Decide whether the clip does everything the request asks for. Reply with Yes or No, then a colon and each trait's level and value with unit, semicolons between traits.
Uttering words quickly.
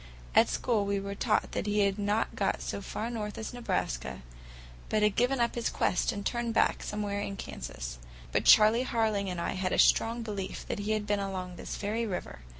Yes: fast, 210 wpm